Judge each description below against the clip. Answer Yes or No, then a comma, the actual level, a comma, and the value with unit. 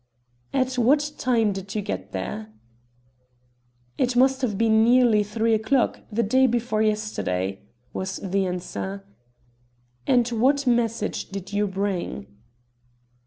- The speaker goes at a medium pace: No, slow, 120 wpm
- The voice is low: No, high, 220 Hz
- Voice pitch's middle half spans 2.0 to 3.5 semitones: No, average, 4.1 semitones